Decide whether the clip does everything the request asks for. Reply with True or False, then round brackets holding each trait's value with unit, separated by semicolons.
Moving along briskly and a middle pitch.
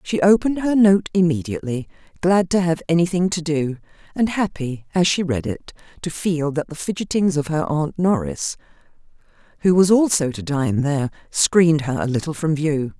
False (175 wpm; 160 Hz)